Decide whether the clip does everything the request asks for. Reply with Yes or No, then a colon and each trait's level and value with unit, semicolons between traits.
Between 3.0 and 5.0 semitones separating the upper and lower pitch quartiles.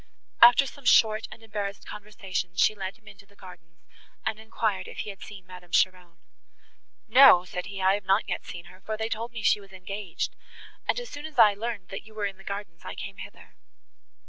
No: narrow, 2.6 semitones